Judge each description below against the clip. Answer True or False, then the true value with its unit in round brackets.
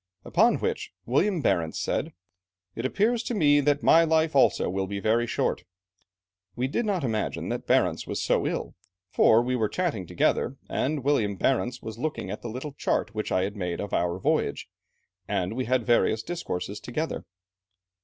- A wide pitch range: True (6.4 semitones)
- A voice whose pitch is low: True (125 Hz)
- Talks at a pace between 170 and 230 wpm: True (175 wpm)